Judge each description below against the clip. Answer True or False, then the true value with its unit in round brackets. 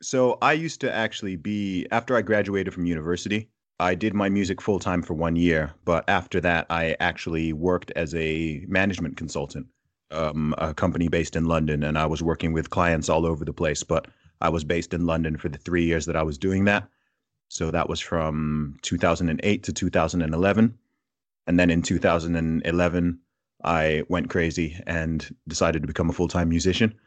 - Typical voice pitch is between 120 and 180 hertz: False (85 Hz)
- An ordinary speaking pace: True (185 wpm)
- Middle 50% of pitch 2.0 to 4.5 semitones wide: True (2.8 semitones)